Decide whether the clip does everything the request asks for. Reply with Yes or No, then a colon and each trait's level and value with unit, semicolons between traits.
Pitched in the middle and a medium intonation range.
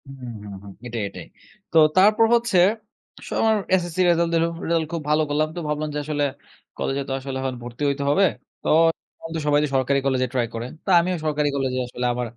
Yes: medium, 145 Hz; average, 4.3 semitones